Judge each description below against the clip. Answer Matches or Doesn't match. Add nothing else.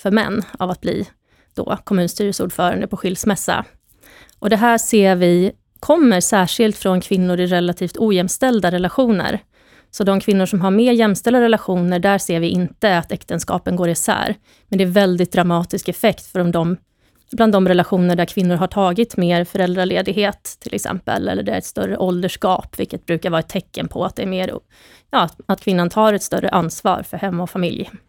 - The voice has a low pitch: Doesn't match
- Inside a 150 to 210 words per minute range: Matches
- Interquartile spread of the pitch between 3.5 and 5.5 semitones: Doesn't match